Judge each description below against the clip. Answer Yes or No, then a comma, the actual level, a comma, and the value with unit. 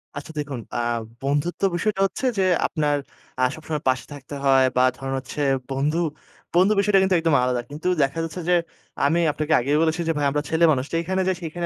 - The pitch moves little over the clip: No, average, 3.8 semitones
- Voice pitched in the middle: Yes, medium, 155 Hz